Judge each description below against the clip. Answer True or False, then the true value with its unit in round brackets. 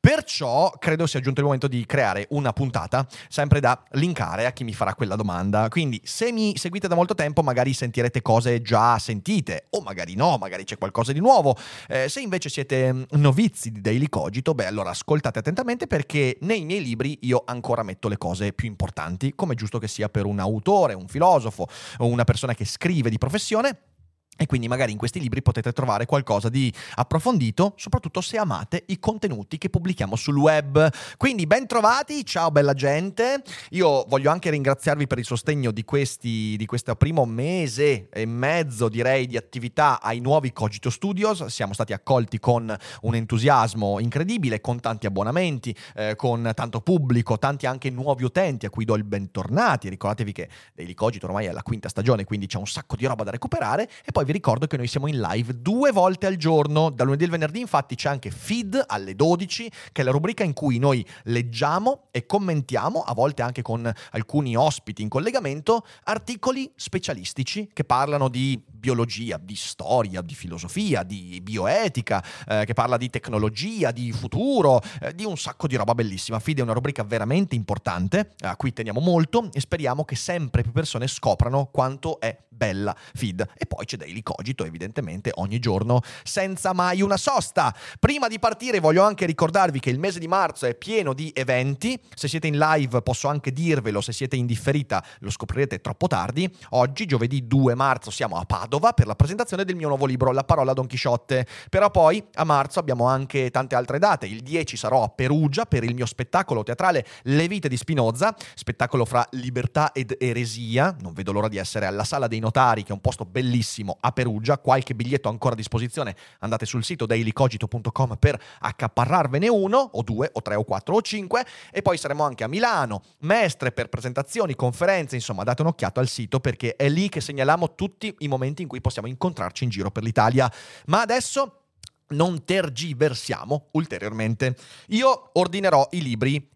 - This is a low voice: True (130 Hz)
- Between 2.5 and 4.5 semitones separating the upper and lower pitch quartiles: False (5.3 semitones)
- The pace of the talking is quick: True (185 wpm)